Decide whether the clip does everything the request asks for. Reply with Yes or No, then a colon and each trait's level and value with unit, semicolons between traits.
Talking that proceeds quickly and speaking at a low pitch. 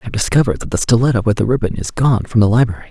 Yes: fast, 290 wpm; low, 115 Hz